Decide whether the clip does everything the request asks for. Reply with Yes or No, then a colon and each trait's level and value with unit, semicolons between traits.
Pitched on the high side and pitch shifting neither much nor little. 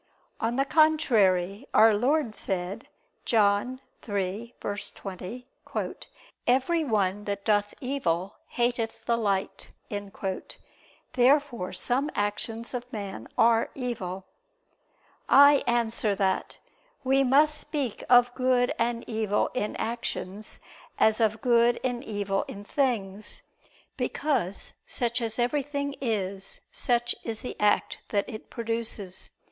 Yes: high, 230 Hz; average, 3.7 semitones